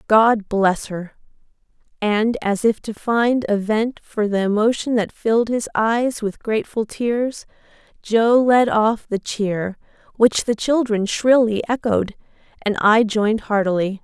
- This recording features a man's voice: No, female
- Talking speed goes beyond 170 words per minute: No, average, 145 wpm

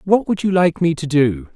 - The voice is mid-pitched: Yes, medium, 160 Hz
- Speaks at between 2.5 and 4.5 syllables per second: No, 5.0 syllables/s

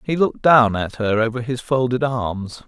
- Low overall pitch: Yes, low, 120 Hz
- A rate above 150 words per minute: Yes, average, 200 wpm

